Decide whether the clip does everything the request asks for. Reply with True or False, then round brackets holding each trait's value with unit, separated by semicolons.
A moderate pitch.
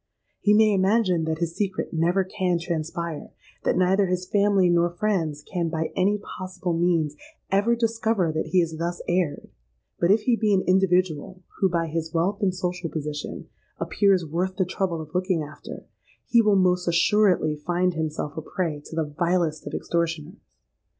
True (180 Hz)